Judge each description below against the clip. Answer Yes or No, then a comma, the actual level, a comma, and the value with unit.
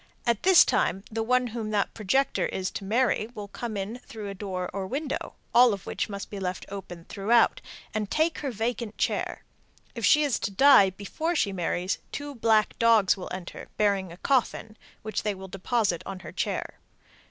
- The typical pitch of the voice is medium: No, high, 215 Hz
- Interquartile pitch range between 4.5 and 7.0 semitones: No, average, 3.7 semitones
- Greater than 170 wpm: Yes, average, 190 wpm